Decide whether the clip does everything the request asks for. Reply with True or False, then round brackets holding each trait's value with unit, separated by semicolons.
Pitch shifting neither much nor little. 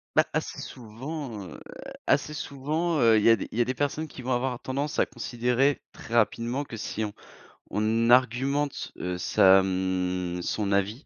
True (4.7 semitones)